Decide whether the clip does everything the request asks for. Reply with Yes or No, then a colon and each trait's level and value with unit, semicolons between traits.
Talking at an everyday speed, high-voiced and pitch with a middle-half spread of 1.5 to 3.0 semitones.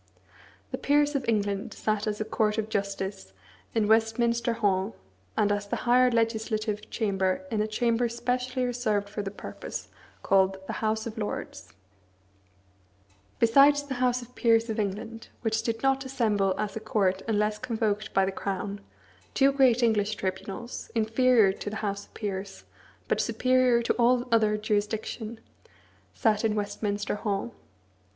Yes: average, 150 wpm; high, 220 Hz; narrow, 2.6 semitones